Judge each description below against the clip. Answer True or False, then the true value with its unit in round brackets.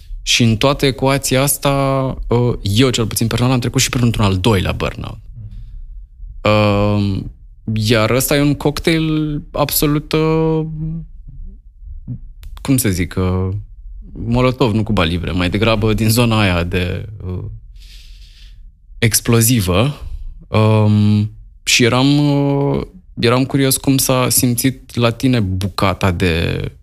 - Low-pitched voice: True (110 Hz)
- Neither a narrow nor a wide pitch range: False (5.9 semitones)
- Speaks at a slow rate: True (105 wpm)